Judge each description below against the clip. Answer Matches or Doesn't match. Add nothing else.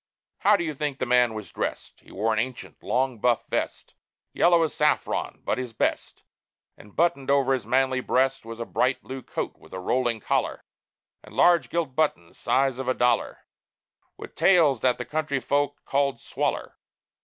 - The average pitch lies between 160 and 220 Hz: Doesn't match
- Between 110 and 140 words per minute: Doesn't match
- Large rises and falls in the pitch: Doesn't match